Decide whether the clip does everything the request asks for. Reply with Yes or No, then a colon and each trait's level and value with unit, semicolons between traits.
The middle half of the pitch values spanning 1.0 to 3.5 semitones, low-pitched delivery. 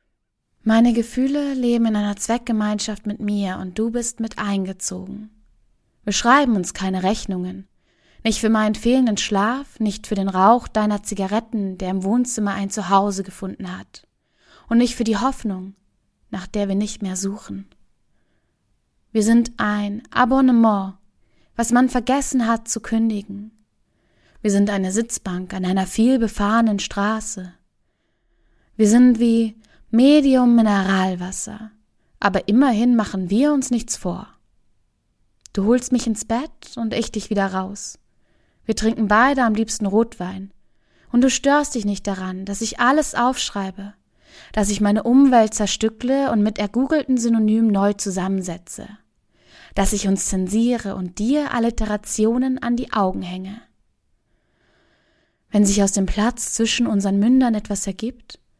No: average, 3.1 semitones; high, 215 Hz